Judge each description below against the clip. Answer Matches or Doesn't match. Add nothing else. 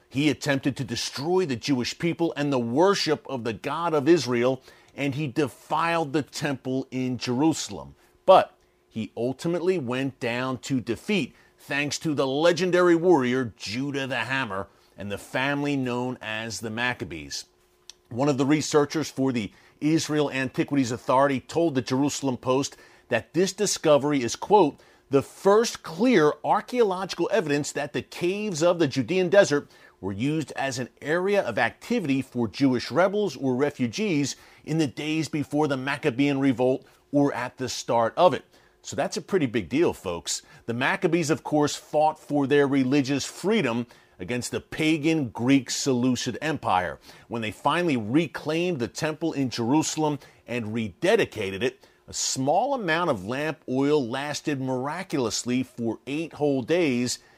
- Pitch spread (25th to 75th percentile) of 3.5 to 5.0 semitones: Matches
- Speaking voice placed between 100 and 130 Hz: Doesn't match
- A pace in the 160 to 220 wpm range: Doesn't match